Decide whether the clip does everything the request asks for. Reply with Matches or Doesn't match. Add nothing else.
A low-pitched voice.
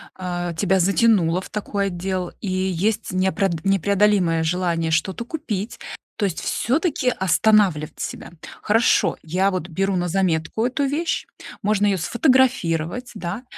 Doesn't match